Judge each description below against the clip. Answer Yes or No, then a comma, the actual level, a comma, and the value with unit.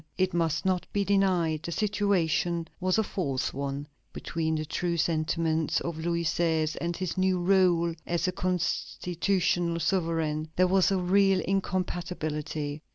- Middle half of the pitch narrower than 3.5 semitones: Yes, narrow, 2.6 semitones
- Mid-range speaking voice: Yes, medium, 170 Hz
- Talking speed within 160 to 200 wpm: No, average, 145 wpm